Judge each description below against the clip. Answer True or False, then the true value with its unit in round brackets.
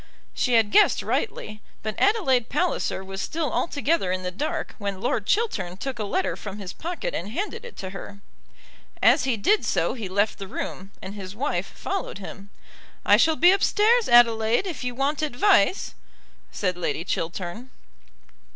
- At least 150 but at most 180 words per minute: True (170 wpm)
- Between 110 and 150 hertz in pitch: False (235 Hz)